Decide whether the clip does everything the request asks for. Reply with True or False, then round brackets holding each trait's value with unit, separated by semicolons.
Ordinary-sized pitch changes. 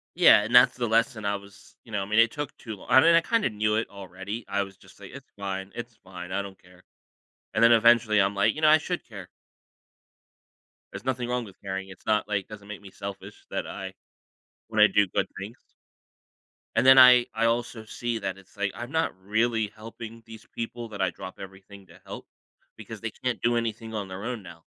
True (3.1 semitones)